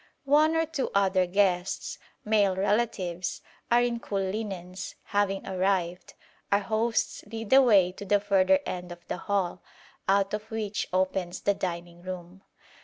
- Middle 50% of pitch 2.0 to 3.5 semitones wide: Yes, average, 2.9 semitones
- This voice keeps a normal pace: Yes, average, 150 wpm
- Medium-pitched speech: No, high, 195 Hz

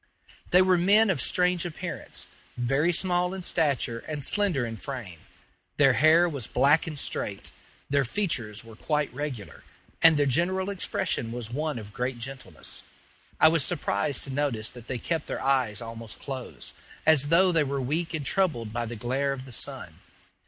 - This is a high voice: No, medium, 140 Hz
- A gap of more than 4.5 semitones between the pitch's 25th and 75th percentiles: Yes, wide, 5.5 semitones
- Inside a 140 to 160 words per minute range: No, average, 175 wpm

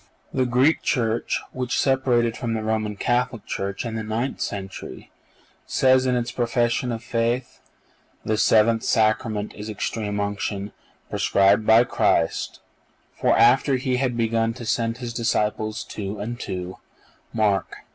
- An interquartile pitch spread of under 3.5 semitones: Yes, narrow, 2.4 semitones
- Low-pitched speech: Yes, low, 115 Hz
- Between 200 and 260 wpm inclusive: No, average, 145 wpm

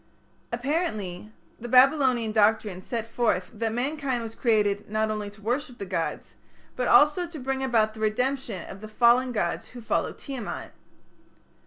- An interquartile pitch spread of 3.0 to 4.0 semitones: Yes, average, 3.3 semitones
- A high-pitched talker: Yes, high, 230 Hz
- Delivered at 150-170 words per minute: Yes, average, 160 wpm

